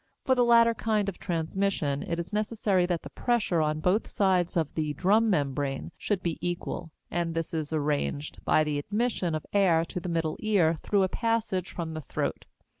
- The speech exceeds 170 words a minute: Yes, average, 190 wpm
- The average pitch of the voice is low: No, medium, 175 Hz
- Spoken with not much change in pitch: No, average, 4.5 semitones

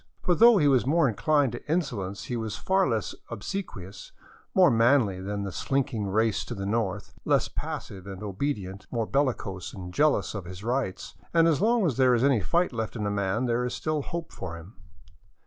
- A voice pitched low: Yes, low, 115 Hz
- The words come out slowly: No, average, 200 wpm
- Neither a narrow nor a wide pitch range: No, wide, 6.4 semitones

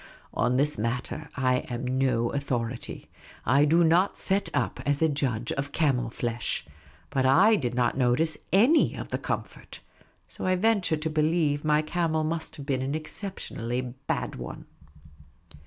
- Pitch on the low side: No, medium, 145 Hz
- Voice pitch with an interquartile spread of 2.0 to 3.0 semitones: No, average, 4.3 semitones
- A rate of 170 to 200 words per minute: No, average, 155 wpm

